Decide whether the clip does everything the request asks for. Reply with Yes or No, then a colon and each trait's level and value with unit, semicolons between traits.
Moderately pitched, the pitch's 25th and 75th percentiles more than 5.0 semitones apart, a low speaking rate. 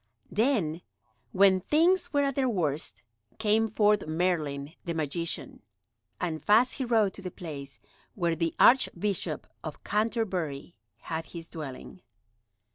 Yes: medium, 180 Hz; wide, 5.6 semitones; slow, 125 wpm